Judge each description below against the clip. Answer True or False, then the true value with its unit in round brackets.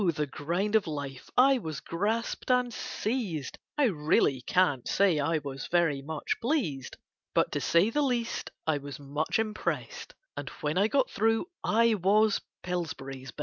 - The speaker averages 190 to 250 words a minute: False (160 wpm)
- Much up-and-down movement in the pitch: True (7.4 semitones)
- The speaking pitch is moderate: True (180 Hz)